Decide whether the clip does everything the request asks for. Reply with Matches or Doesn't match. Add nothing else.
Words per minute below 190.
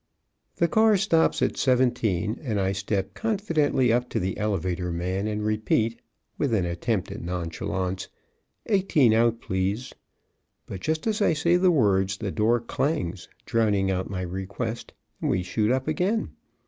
Matches